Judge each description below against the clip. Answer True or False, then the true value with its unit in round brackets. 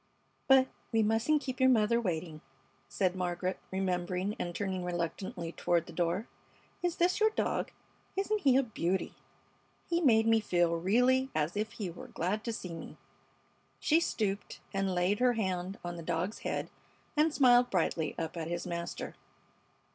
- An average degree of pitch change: False (5.8 semitones)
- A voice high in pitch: True (195 Hz)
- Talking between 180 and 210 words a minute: False (160 wpm)